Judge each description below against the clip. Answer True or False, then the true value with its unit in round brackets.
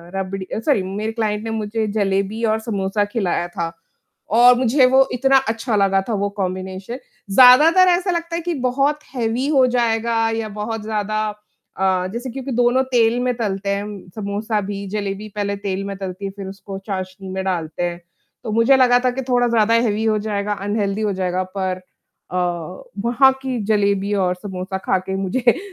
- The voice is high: True (210 Hz)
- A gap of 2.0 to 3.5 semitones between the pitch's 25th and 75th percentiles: False (3.9 semitones)